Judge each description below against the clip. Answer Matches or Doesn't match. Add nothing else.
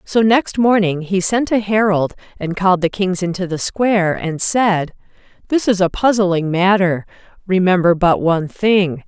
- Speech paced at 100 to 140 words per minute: Doesn't match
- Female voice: Matches